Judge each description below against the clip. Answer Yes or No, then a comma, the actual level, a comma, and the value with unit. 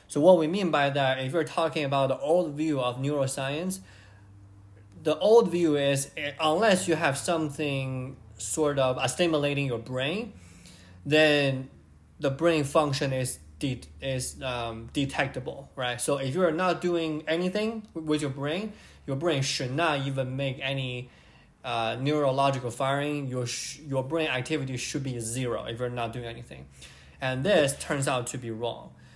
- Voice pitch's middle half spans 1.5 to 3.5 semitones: No, average, 3.9 semitones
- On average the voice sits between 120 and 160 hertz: Yes, low, 135 Hz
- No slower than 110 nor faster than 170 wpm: Yes, average, 160 wpm